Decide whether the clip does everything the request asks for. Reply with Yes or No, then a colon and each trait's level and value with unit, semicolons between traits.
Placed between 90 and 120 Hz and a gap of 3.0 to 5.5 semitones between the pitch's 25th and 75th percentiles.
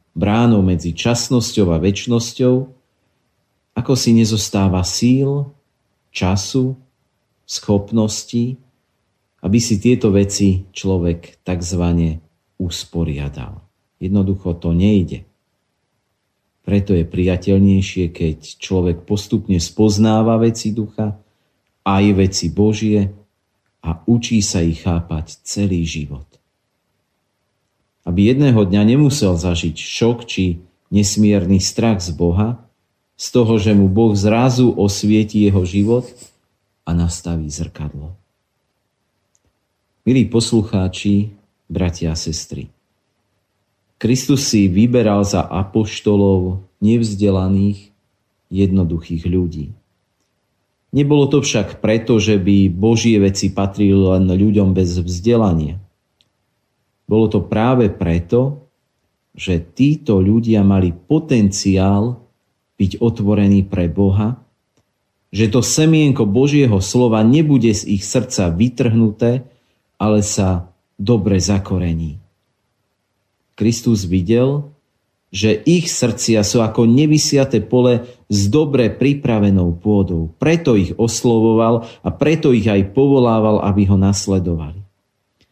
Yes: low, 100 Hz; average, 3.6 semitones